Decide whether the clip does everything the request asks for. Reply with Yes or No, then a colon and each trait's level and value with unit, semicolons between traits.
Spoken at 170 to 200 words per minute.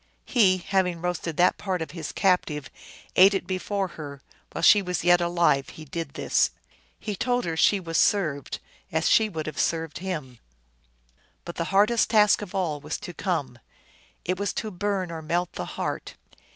Yes: average, 180 wpm